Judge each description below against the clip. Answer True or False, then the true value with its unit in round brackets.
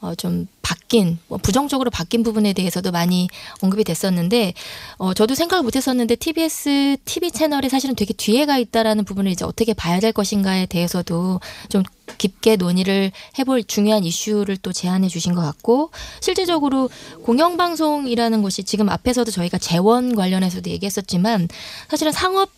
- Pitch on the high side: True (215 Hz)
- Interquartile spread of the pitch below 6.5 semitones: True (5.8 semitones)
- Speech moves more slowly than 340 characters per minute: False (375 characters per minute)